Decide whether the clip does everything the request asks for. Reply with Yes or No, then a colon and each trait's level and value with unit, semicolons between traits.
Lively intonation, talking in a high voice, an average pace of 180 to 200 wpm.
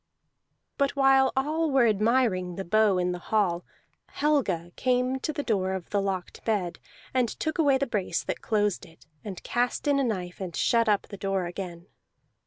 Yes: wide, 6.2 semitones; high, 215 Hz; average, 185 wpm